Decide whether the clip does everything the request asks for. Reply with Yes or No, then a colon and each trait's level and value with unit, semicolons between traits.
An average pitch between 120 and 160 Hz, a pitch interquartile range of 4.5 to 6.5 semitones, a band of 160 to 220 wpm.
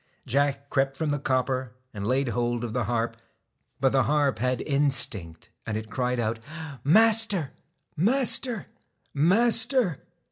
No: low, 135 Hz; average, 4.9 semitones; slow, 135 wpm